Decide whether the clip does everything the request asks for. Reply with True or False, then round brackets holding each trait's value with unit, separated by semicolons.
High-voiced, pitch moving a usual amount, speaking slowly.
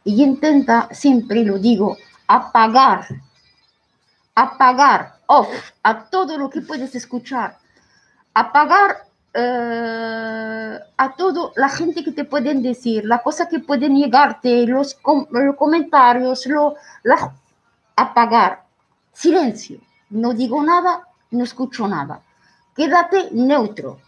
True (265 Hz; 3.9 semitones; 110 wpm)